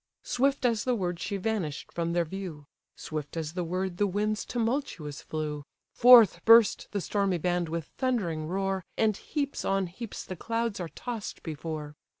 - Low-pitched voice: No, high, 190 Hz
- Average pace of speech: Yes, average, 165 wpm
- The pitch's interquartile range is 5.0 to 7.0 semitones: Yes, average, 5.3 semitones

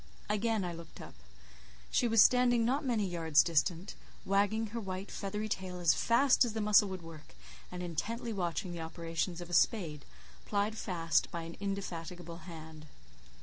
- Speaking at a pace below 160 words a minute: No, average, 165 wpm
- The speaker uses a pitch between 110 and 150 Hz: No, medium, 185 Hz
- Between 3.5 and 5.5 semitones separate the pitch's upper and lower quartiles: Yes, average, 4.5 semitones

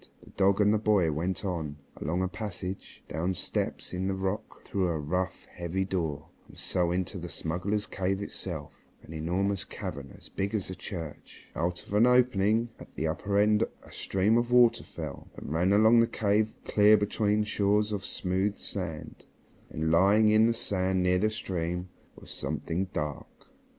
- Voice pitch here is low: Yes, very low, 95 Hz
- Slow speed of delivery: No, average, 180 wpm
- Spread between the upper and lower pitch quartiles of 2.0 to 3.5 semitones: Yes, average, 3.1 semitones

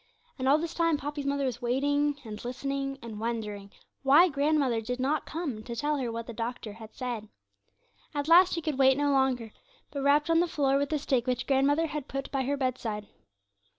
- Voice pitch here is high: Yes, very high, 275 Hz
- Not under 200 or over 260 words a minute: Yes, fast, 205 wpm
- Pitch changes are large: No, average, 3.4 semitones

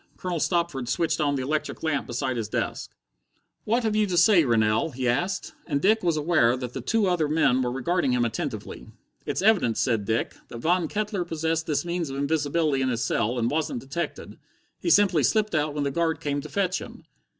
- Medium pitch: Yes, medium, 155 Hz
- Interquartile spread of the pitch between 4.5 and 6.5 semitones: Yes, average, 5.3 semitones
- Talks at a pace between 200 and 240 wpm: Yes, fast, 205 wpm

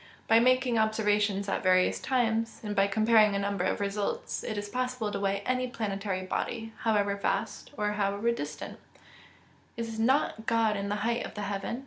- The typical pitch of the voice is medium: No, high, 210 Hz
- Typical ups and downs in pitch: No, narrow, 2.3 semitones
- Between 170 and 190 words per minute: Yes, average, 180 wpm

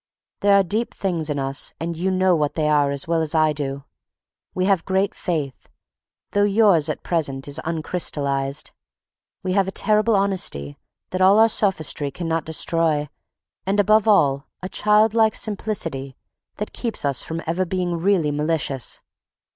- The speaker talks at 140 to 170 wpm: Yes, average, 160 wpm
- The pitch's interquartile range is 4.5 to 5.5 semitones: Yes, average, 5.0 semitones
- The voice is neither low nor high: Yes, medium, 170 Hz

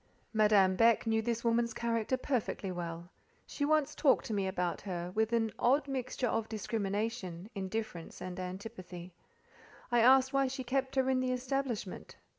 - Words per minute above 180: No, average, 160 wpm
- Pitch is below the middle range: No, high, 225 Hz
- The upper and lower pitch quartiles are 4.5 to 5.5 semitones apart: Yes, average, 5.1 semitones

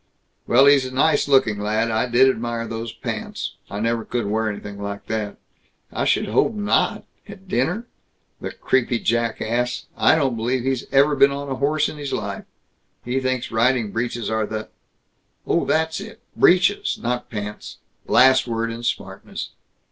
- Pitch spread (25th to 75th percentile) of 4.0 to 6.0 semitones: No, average, 3.6 semitones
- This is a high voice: No, low, 120 Hz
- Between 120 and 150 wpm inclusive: No, average, 175 wpm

